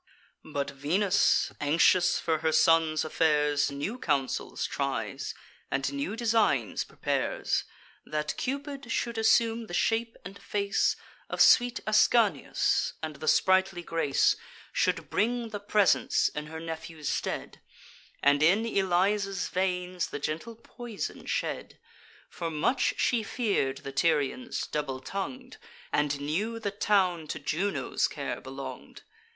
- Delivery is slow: Yes, slow, 125 wpm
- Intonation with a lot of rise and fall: Yes, wide, 6.1 semitones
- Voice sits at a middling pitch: Yes, medium, 180 Hz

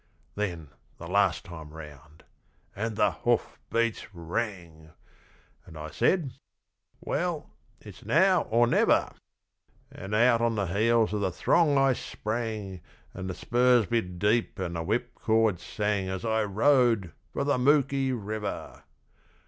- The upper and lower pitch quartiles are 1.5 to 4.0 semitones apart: No, average, 4.7 semitones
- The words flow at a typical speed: No, slow, 130 wpm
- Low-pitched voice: Yes, low, 110 Hz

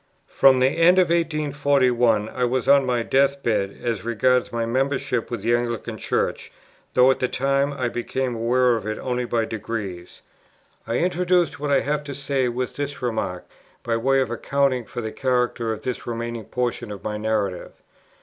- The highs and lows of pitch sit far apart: No, average, 3.2 semitones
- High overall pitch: No, low, 125 Hz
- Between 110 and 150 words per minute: No, average, 180 wpm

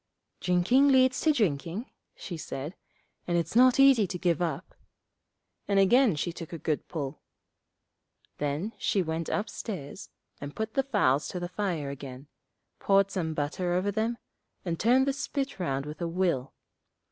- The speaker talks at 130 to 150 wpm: No, average, 160 wpm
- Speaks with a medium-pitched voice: Yes, medium, 180 Hz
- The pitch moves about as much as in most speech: No, wide, 6.0 semitones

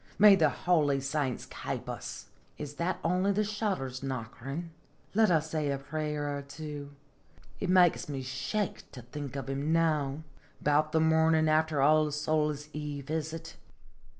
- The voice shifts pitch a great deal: No, narrow, 2.4 semitones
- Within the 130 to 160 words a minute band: Yes, average, 155 wpm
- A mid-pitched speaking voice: Yes, medium, 150 Hz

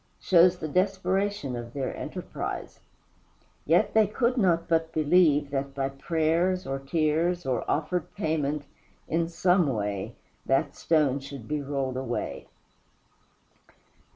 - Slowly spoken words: Yes, slow, 125 wpm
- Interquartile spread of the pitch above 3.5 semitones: Yes, average, 4.5 semitones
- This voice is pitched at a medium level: Yes, medium, 155 Hz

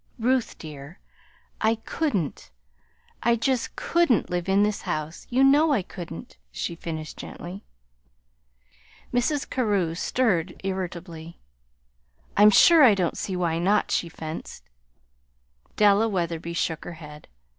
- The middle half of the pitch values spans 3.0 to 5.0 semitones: No, wide, 5.5 semitones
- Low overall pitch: No, high, 190 Hz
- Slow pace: Yes, slow, 125 wpm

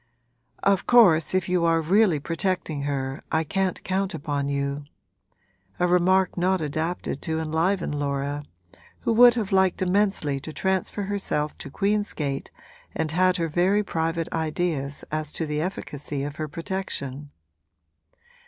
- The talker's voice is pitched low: No, medium, 165 Hz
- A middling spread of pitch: Yes, average, 4.4 semitones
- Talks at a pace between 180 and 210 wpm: No, average, 145 wpm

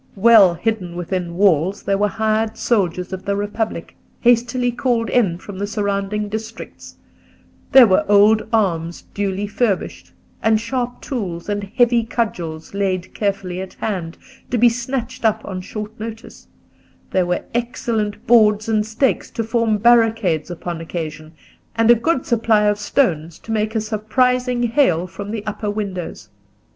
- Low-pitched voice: No, high, 210 Hz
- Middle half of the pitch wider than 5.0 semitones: No, average, 3.4 semitones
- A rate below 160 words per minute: Yes, average, 150 wpm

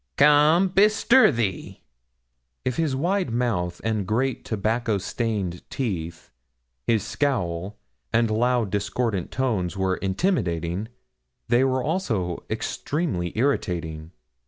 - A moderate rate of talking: No, slow, 105 wpm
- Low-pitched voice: Yes, low, 115 Hz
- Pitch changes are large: Yes, wide, 6.3 semitones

